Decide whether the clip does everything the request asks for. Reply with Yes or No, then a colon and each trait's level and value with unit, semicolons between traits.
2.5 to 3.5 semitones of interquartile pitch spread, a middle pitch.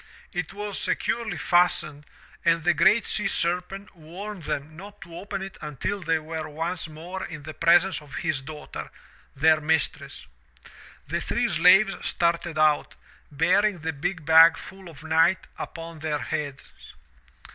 Yes: average, 3.2 semitones; medium, 165 Hz